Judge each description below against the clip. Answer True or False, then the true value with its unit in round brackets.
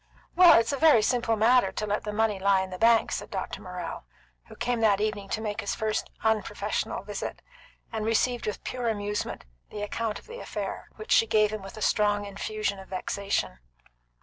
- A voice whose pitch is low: False (215 Hz)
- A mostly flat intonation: True (2.1 semitones)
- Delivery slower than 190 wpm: False (200 wpm)